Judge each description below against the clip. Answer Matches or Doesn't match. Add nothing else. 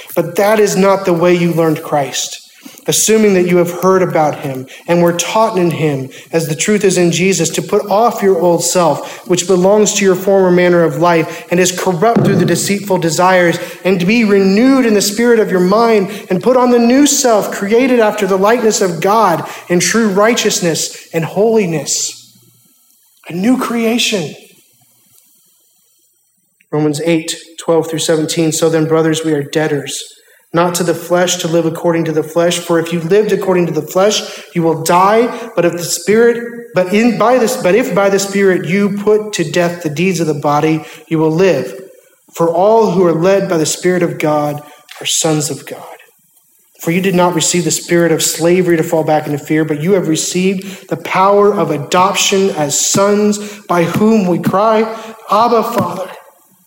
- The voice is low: Doesn't match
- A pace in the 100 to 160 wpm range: Doesn't match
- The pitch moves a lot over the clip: Doesn't match